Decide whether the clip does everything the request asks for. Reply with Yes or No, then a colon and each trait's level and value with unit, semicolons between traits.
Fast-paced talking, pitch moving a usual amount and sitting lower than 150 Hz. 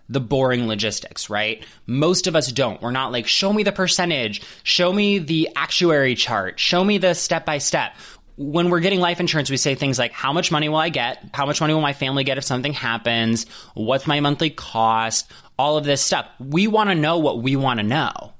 No: fast, 220 wpm; wide, 5.9 semitones; medium, 140 Hz